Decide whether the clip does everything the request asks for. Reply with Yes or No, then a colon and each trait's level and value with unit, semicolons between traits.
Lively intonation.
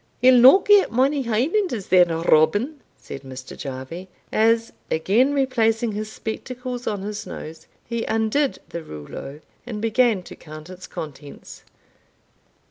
Yes: wide, 7.3 semitones